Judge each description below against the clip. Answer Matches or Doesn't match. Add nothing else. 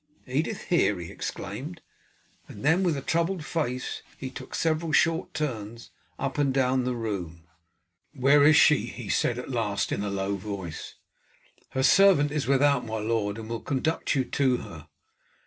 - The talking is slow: Doesn't match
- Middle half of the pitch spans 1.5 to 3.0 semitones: Doesn't match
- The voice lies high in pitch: Doesn't match